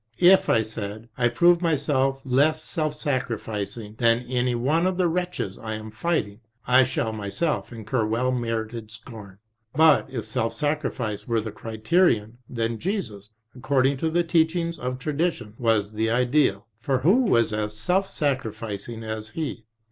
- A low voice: Yes, low, 125 Hz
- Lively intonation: Yes, wide, 5.7 semitones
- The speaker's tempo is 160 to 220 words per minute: No, average, 150 wpm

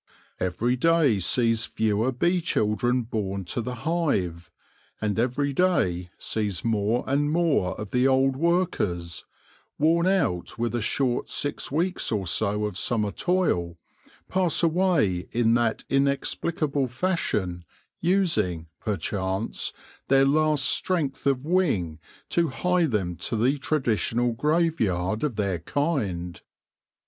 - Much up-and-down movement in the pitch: Yes, wide, 7.3 semitones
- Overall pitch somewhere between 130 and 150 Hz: No, low, 120 Hz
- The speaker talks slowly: Yes, slow, 130 wpm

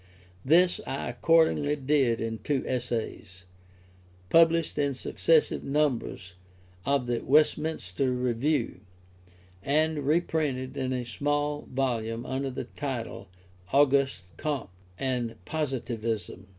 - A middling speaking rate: No, slow, 100 wpm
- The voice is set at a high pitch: No, low, 135 Hz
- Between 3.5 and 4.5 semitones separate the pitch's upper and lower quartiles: Yes, average, 3.8 semitones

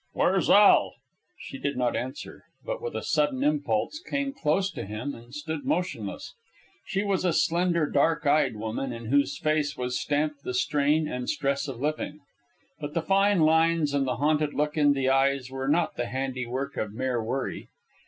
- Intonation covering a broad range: No, average, 3.4 semitones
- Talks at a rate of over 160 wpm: Yes, average, 180 wpm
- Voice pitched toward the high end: No, medium, 145 Hz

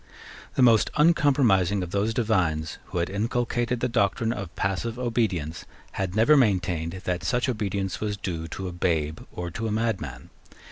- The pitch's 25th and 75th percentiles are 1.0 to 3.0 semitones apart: No, average, 4.8 semitones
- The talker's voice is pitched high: No, low, 100 Hz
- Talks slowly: No, average, 160 wpm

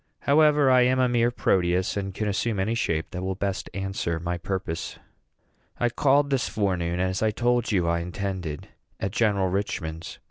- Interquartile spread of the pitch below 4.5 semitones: No, average, 4.9 semitones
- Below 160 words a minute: No, average, 175 wpm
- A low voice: Yes, very low, 95 Hz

